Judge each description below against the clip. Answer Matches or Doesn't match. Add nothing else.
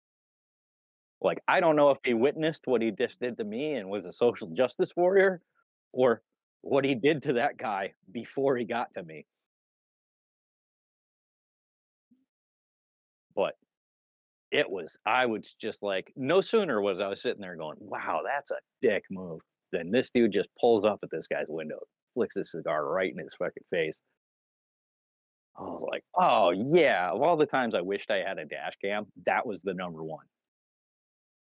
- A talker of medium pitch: Matches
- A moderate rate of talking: Matches